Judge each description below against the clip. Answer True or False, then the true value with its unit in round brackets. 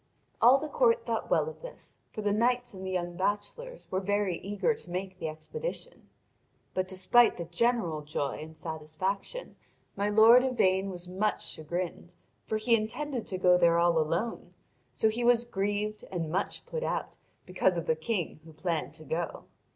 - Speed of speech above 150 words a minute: True (175 wpm)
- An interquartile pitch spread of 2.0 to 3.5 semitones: False (5.1 semitones)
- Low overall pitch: False (190 Hz)